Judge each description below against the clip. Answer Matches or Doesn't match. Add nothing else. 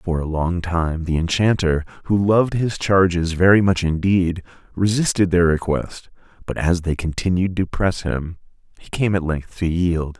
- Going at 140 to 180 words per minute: Matches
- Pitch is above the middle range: Doesn't match